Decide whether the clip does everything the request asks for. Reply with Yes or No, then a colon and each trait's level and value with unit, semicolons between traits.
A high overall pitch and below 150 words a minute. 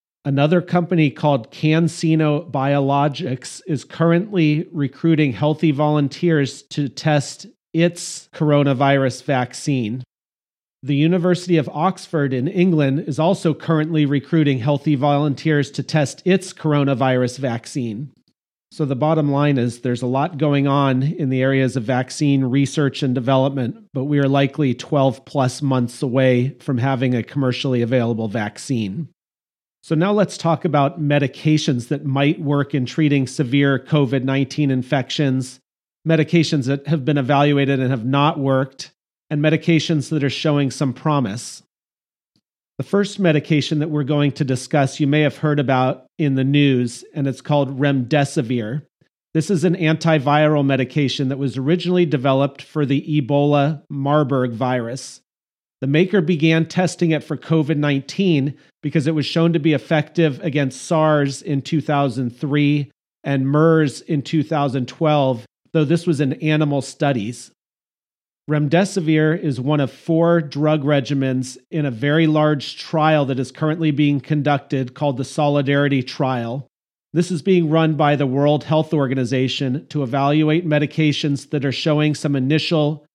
No: medium, 145 Hz; average, 140 wpm